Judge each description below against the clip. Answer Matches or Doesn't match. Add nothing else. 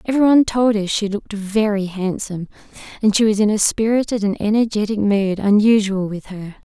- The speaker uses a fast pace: Doesn't match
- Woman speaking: Matches